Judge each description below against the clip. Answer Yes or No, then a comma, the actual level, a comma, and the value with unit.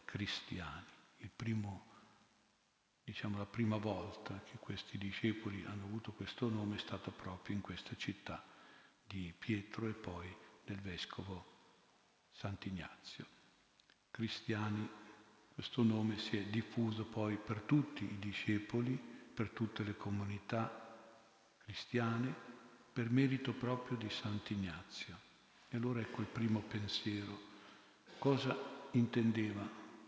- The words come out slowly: Yes, slow, 110 wpm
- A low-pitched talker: Yes, low, 110 Hz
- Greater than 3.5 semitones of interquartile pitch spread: No, narrow, 2.4 semitones